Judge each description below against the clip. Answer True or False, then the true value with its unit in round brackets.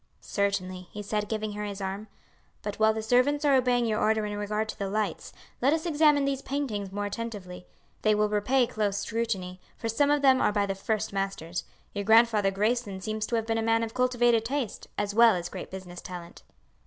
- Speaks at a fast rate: True (210 wpm)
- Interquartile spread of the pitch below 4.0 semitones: True (2.8 semitones)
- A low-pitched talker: False (215 Hz)